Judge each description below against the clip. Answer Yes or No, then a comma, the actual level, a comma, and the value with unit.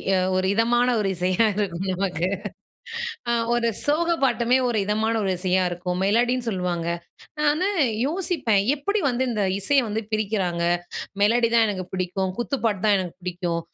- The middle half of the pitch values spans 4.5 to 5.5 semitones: Yes, average, 4.8 semitones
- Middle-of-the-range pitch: No, high, 210 Hz